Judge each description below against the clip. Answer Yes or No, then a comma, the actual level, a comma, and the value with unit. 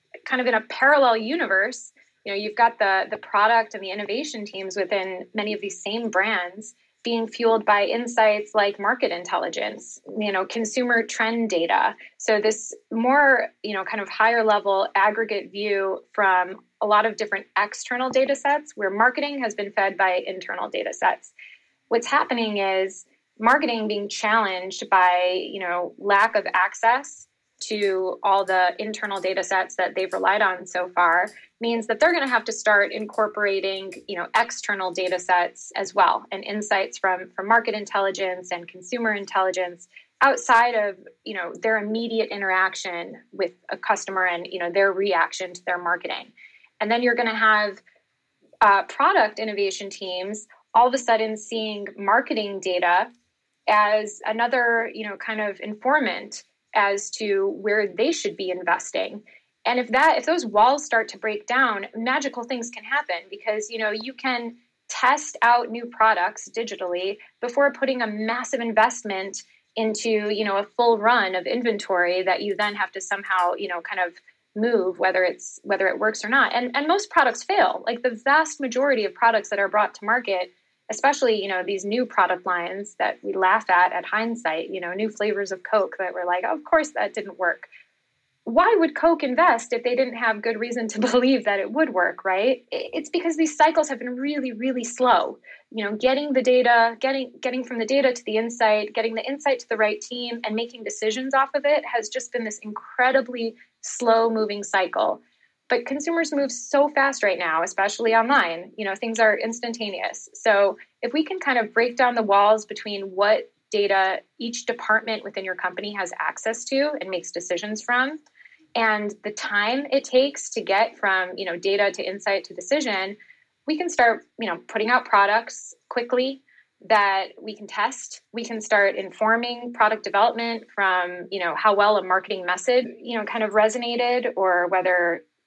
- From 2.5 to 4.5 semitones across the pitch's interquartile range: Yes, average, 3.7 semitones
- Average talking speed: Yes, average, 180 wpm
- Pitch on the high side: Yes, high, 220 Hz